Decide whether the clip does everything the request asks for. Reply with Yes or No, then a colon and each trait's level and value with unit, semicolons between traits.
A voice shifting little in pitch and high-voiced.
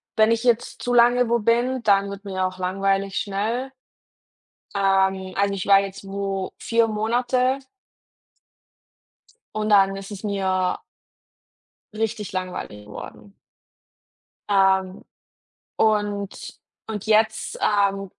Yes: narrow, 2.3 semitones; high, 200 Hz